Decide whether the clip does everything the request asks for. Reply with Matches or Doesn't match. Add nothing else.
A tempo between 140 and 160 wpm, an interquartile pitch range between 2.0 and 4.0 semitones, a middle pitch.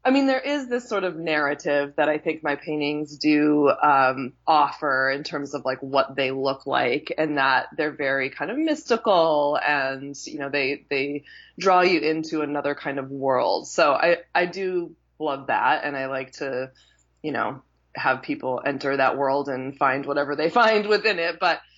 Doesn't match